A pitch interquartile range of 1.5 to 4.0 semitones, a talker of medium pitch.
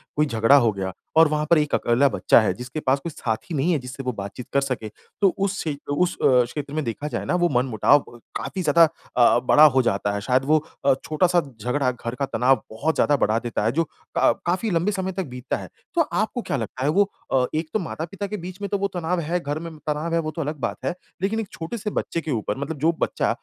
No: average, 5.0 semitones; medium, 150 Hz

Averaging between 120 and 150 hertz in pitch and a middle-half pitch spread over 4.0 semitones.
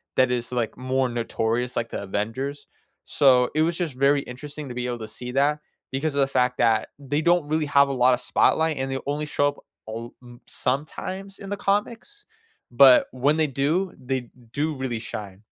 No: low, 135 Hz; average, 3.4 semitones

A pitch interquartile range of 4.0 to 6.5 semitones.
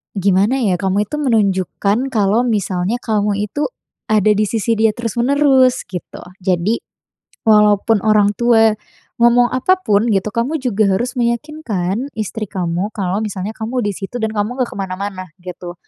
No: average, 3.4 semitones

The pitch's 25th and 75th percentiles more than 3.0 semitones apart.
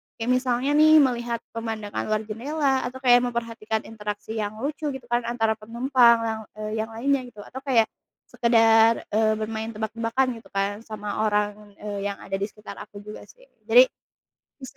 No: narrow, 2.5 semitones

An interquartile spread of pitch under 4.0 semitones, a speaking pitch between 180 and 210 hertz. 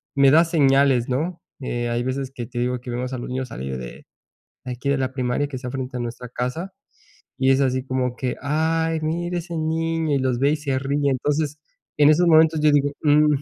No: average, 3.5 semitones; low, 135 Hz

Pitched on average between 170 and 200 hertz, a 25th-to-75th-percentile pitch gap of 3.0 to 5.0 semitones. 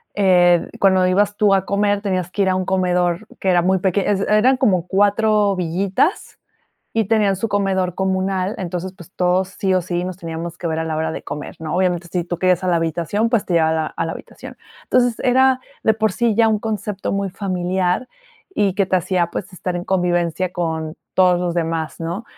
No: medium, 185 Hz; narrow, 2.6 semitones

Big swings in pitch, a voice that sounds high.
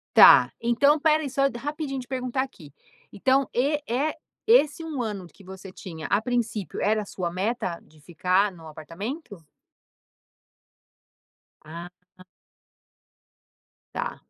Yes: wide, 7.0 semitones; high, 230 Hz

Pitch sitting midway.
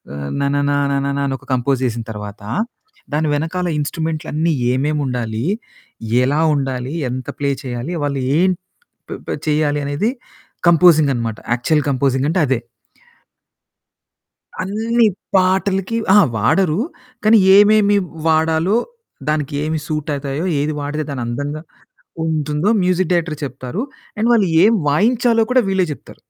Yes: medium, 150 Hz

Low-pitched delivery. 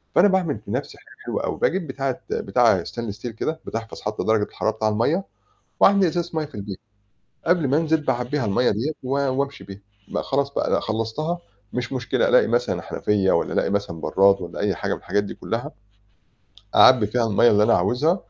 Yes: low, 125 Hz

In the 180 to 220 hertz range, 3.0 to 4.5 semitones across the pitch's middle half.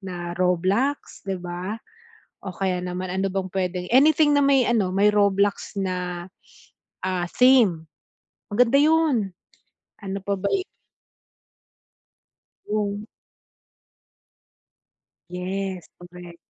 Yes: high, 195 Hz; average, 3.4 semitones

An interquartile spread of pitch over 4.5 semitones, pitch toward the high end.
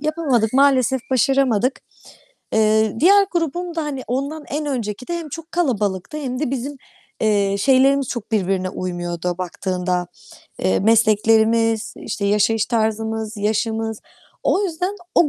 Yes: average, 5.1 semitones; high, 230 Hz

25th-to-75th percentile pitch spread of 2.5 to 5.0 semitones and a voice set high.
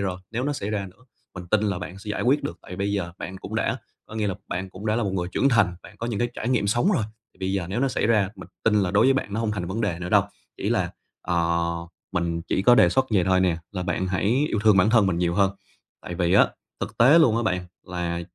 No: average, 3.9 semitones; low, 100 Hz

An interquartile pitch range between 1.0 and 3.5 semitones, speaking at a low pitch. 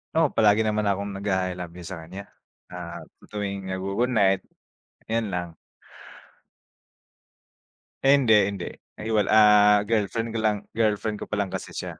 Yes: narrow, 2.5 semitones; low, 105 Hz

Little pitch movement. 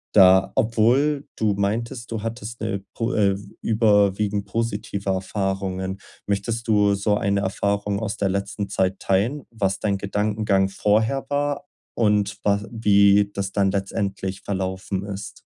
Yes: narrow, 2.1 semitones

